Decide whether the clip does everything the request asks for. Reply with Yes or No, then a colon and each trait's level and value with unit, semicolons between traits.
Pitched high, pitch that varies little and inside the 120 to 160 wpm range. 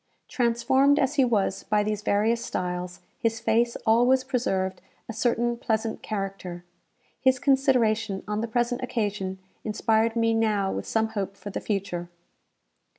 No: high, 225 Hz; average, 3.0 semitones; average, 145 wpm